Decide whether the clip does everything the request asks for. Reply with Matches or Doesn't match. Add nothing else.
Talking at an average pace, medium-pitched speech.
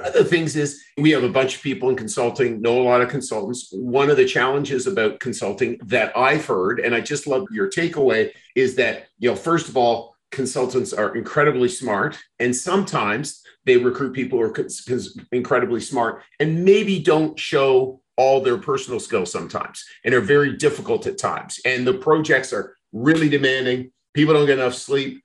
Matches